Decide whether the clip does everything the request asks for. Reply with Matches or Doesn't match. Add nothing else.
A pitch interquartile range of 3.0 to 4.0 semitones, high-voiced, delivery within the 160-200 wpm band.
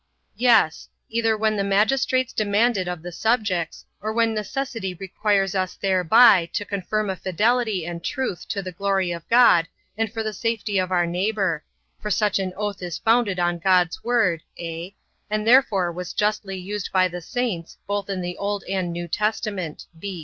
Matches